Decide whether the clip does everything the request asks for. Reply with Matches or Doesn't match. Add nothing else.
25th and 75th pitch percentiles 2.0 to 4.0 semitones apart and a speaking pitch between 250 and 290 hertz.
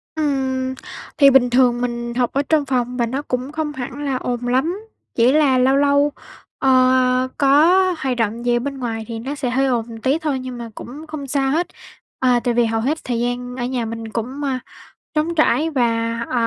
Matches